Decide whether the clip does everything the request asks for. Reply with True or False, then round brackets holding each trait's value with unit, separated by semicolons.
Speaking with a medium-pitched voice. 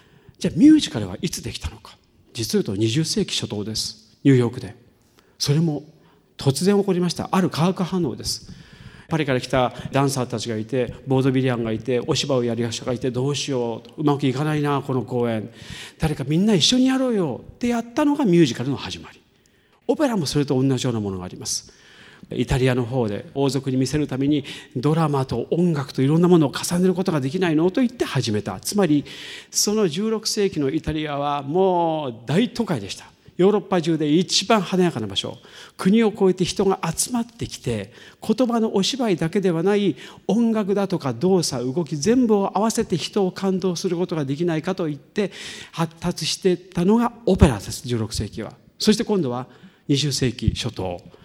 True (155 Hz)